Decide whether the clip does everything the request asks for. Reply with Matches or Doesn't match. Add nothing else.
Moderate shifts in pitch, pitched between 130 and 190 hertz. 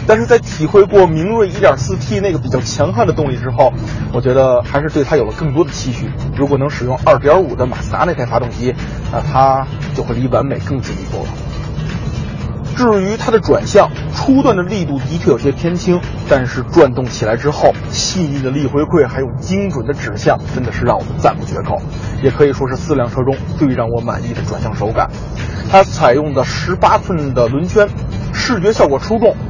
Matches